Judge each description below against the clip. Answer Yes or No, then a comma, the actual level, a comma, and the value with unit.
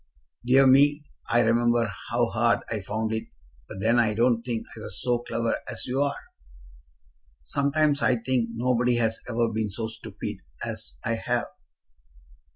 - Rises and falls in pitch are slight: Yes, narrow, 2.1 semitones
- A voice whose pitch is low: Yes, low, 120 Hz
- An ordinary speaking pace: Yes, average, 160 wpm